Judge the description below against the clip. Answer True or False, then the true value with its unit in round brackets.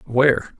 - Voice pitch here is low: True (130 Hz)